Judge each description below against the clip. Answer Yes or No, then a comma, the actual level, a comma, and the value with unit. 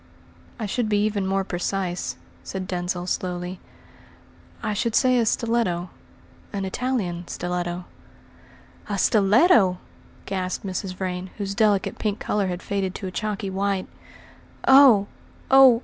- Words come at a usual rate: No, slow, 130 wpm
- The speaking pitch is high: Yes, high, 195 Hz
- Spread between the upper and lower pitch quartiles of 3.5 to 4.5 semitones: No, average, 2.8 semitones